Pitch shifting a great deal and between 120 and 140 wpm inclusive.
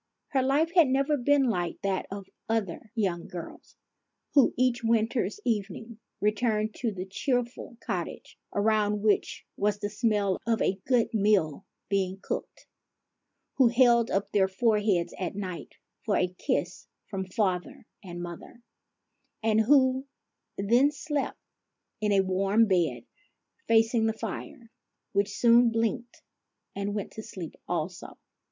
No: average, 3.5 semitones; slow, 135 wpm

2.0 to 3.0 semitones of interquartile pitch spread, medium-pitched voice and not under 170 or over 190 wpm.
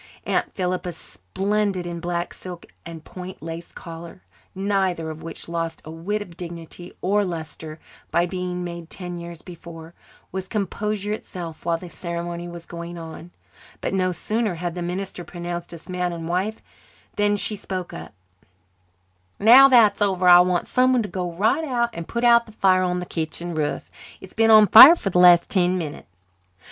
Yes: average, 2.7 semitones; medium, 180 Hz; average, 175 wpm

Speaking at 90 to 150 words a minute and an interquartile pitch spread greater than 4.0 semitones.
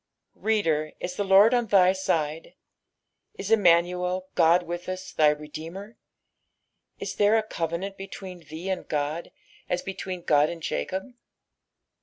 No: average, 140 wpm; average, 2.9 semitones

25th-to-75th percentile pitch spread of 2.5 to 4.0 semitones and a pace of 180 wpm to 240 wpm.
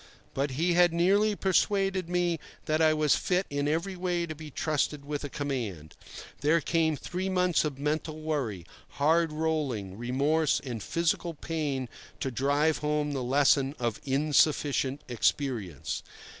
No: average, 3.5 semitones; average, 145 wpm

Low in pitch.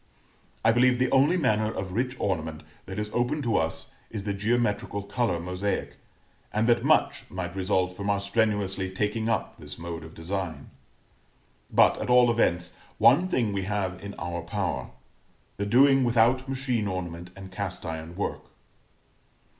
Yes: low, 100 Hz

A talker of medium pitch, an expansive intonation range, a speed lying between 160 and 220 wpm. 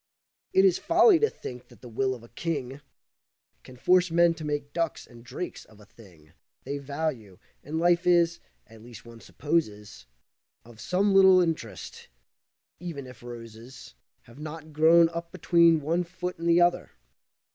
Yes: medium, 155 Hz; wide, 6.3 semitones; average, 165 wpm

